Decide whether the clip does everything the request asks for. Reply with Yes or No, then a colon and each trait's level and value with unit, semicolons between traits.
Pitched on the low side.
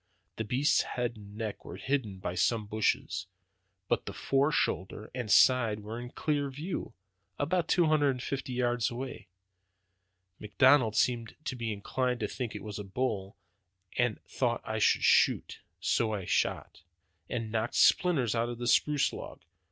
Yes: low, 120 Hz